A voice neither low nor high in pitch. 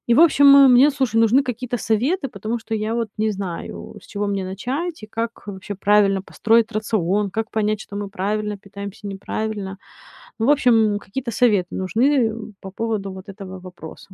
No: high, 215 Hz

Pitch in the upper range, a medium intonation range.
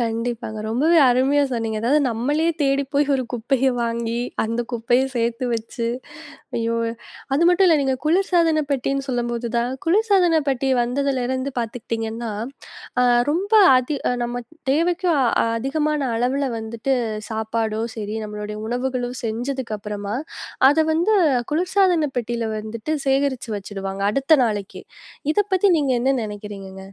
Yes: high, 245 Hz; average, 4.3 semitones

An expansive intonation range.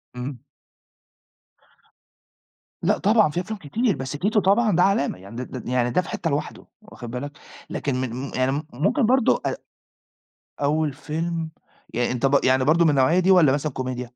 Yes: wide, 5.8 semitones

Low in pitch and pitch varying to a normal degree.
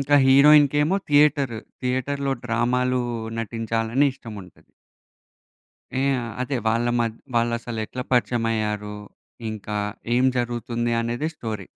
Yes: low, 120 Hz; average, 3.2 semitones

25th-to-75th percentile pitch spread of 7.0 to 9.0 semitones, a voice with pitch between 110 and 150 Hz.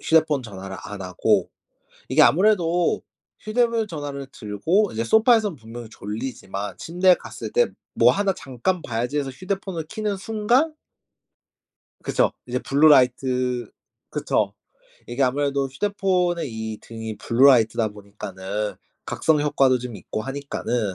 Yes: wide, 8.3 semitones; low, 135 Hz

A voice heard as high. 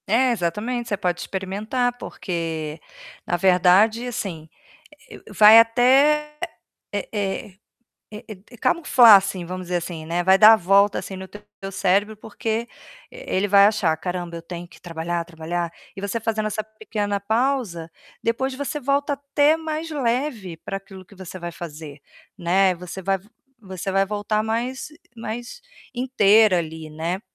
Yes: high, 200 Hz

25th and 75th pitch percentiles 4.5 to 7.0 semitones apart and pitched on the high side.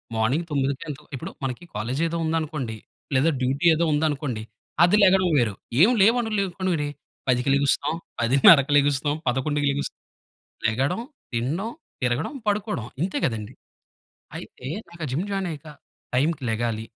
No: average, 5.0 semitones; medium, 145 Hz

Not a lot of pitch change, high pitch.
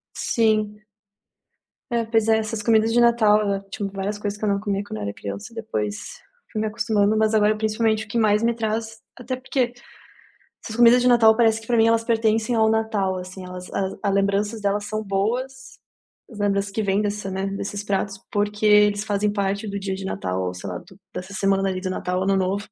Yes: narrow, 2.2 semitones; high, 210 Hz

